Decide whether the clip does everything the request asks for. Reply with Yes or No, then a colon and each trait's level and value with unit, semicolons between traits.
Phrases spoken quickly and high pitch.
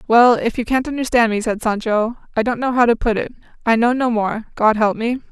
Yes: fast, 250 wpm; high, 230 Hz